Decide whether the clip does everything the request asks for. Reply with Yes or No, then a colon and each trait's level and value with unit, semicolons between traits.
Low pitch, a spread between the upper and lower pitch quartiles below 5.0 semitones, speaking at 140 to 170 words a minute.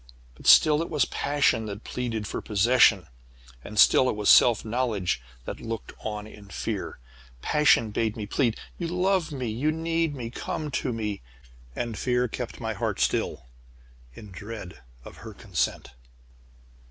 No: low, 115 Hz; wide, 5.4 semitones; average, 155 wpm